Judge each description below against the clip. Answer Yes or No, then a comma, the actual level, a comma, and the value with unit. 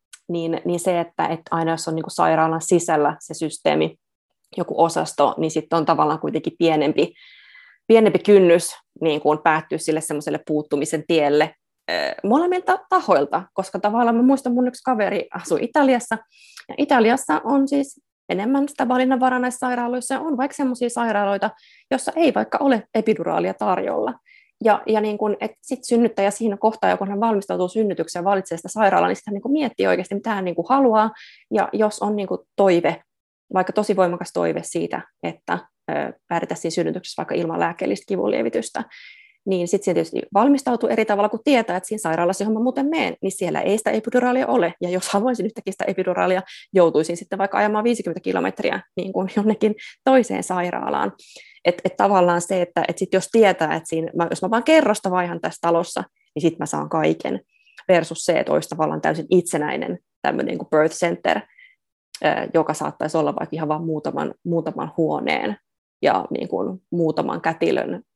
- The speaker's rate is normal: No, fast, 170 wpm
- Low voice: No, high, 200 Hz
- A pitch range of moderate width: No, wide, 6.4 semitones